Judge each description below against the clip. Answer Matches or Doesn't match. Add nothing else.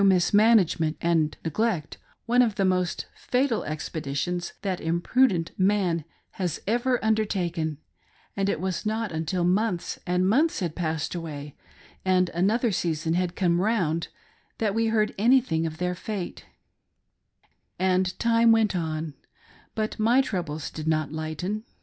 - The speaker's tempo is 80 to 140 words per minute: Matches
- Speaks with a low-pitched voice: Doesn't match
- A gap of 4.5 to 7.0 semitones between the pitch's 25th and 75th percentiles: Matches